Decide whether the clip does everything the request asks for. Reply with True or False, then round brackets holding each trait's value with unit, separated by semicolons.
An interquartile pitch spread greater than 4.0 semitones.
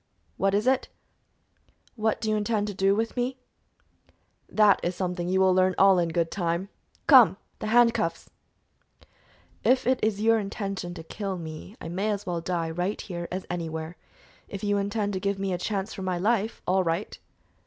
False (3.1 semitones)